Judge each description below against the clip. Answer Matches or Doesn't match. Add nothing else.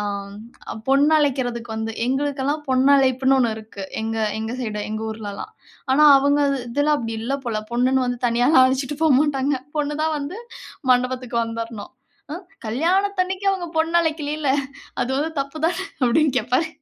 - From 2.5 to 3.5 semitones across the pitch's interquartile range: Doesn't match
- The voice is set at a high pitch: Matches